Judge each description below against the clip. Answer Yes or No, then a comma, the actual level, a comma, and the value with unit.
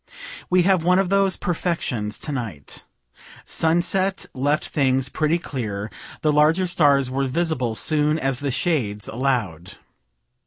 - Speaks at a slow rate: Yes, slow, 130 wpm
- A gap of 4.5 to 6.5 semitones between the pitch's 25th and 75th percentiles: Yes, wide, 5.4 semitones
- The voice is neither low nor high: Yes, medium, 145 Hz